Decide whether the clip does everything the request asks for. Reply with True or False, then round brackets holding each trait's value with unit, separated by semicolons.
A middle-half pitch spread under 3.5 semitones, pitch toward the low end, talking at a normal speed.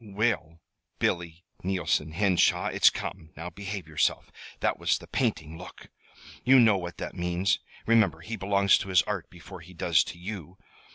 True (3.0 semitones; 90 Hz; 165 wpm)